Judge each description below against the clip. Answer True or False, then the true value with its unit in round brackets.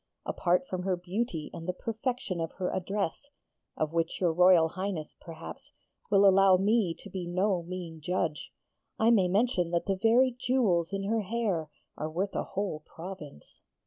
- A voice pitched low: False (185 Hz)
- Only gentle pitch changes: False (3.3 semitones)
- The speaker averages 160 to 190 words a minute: True (170 wpm)